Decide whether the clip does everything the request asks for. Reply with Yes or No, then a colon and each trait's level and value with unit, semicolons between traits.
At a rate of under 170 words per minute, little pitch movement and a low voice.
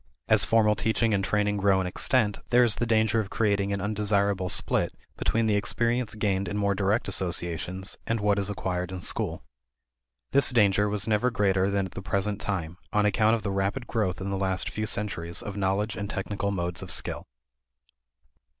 No: average, 190 wpm; narrow, 1.9 semitones; low, 100 Hz